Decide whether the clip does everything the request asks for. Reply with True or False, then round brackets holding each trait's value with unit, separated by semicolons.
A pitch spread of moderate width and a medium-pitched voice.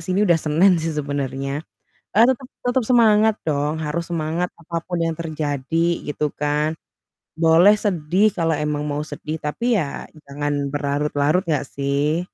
True (3.3 semitones; 155 Hz)